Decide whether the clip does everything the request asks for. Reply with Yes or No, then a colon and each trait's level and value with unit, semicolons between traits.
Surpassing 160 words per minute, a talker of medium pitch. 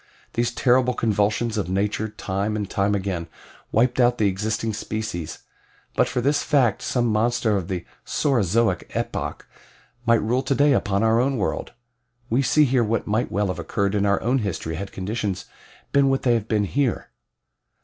No: average, 170 wpm; low, 110 Hz